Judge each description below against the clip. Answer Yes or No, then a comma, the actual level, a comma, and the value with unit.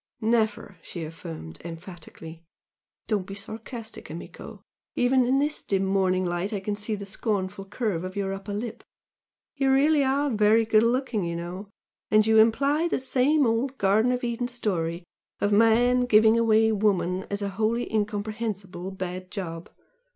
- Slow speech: No, average, 160 wpm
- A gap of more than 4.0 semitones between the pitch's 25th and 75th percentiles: No, average, 3.7 semitones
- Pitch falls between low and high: No, high, 210 Hz